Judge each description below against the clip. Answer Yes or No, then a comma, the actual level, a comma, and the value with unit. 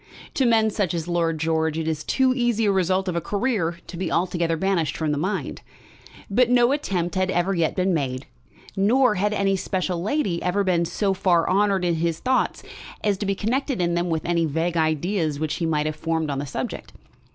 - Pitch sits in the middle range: Yes, medium, 180 Hz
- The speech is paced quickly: Yes, fast, 210 wpm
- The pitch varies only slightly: No, average, 3.6 semitones